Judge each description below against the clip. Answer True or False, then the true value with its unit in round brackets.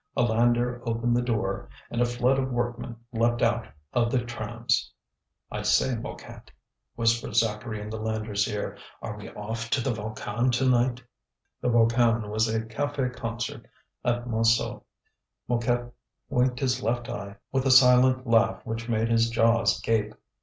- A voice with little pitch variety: True (1.4 semitones)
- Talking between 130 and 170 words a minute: True (160 wpm)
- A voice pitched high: False (115 Hz)